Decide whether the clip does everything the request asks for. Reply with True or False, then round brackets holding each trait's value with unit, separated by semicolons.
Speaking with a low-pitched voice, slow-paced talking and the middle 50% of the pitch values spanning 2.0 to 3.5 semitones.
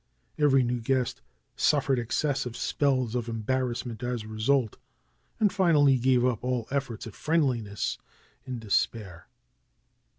True (125 Hz; 125 wpm; 3.1 semitones)